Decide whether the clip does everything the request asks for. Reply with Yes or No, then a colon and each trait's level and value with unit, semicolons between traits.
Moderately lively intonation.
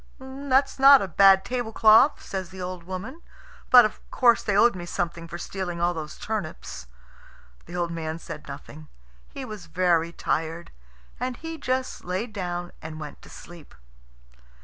No: wide, 5.9 semitones